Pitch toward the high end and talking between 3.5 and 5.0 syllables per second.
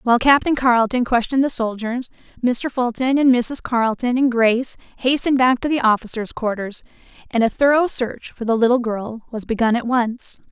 No: high, 240 Hz; 5.4 syllables/s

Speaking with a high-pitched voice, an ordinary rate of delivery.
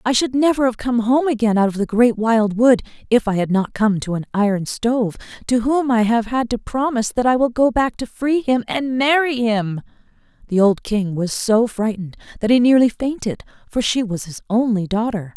No: high, 230 Hz; fast, 220 wpm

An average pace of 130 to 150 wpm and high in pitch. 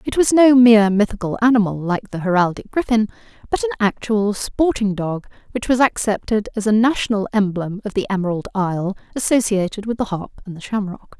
No: average, 175 wpm; high, 210 Hz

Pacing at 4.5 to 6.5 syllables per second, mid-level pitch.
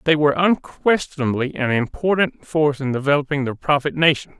Yes: 5.7 syllables/s; medium, 145 Hz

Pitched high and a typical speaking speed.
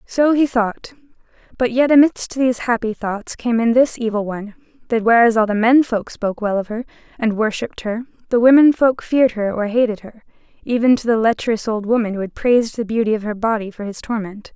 No: high, 230 Hz; fast, 215 wpm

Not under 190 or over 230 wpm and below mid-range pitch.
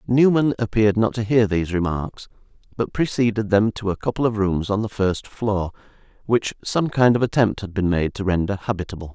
Yes: average, 195 wpm; low, 105 Hz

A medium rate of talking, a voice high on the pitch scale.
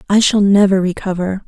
Yes: average, 165 wpm; high, 195 Hz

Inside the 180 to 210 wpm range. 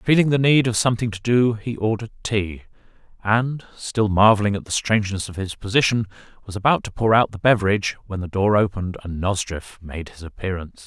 Yes: average, 195 wpm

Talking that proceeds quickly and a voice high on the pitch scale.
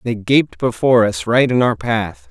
No: fast, 210 wpm; low, 110 Hz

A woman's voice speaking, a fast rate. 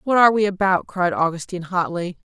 No: female; average, 180 wpm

